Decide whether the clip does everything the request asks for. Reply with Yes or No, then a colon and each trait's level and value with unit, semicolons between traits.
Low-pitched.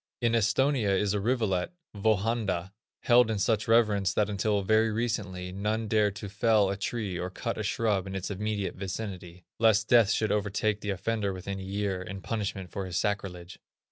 Yes: low, 105 Hz